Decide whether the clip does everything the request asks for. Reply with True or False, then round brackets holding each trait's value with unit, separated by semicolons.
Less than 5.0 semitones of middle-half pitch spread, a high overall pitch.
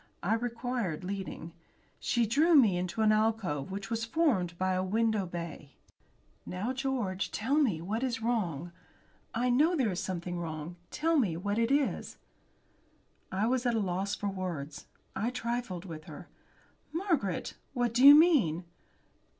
False (5.5 semitones; 215 Hz)